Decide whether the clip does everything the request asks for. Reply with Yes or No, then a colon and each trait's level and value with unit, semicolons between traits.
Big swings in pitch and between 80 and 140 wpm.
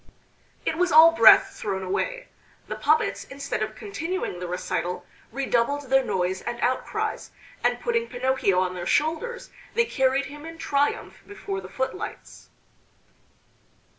Yes: wide, 7.4 semitones; slow, 135 wpm